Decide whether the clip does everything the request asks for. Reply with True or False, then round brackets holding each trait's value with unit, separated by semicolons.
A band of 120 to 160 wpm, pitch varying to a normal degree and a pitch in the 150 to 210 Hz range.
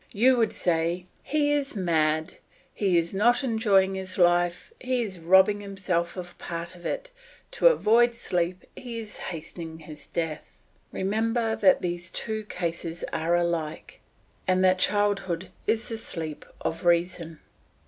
True (145 wpm; 4.3 semitones; 185 Hz)